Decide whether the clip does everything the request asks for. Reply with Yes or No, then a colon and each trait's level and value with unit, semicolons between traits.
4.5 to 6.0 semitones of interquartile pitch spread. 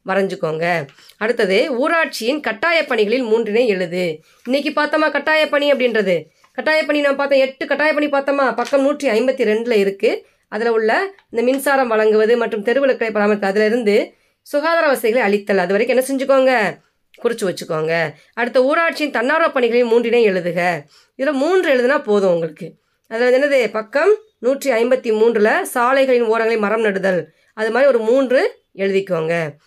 Yes: average, 5.2 semitones